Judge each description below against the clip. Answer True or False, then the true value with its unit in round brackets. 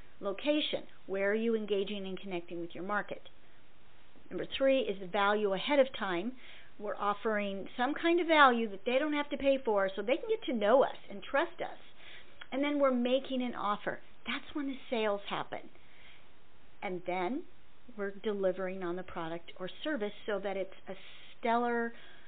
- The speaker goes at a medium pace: True (180 wpm)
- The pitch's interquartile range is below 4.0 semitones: False (5.6 semitones)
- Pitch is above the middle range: True (210 Hz)